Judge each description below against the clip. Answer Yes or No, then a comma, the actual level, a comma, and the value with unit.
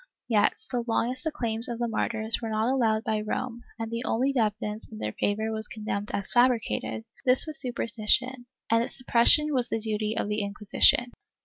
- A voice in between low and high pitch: No, high, 225 Hz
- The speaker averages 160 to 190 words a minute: No, average, 200 wpm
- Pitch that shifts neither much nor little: No, narrow, 2.3 semitones